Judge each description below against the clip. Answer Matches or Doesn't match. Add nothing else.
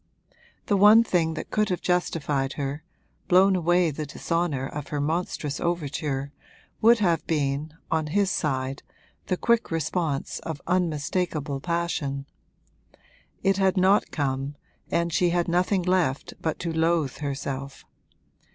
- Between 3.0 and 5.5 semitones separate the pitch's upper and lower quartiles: Matches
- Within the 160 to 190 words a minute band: Doesn't match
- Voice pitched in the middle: Matches